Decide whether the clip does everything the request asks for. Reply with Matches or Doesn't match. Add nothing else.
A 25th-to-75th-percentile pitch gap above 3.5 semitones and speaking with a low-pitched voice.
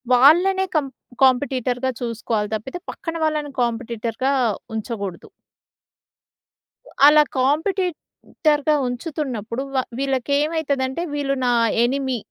Doesn't match